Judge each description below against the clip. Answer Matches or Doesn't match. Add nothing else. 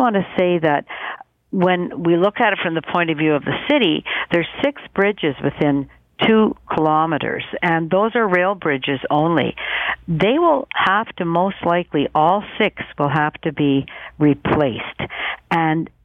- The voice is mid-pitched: Matches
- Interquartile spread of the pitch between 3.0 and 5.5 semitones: Matches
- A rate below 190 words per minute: Matches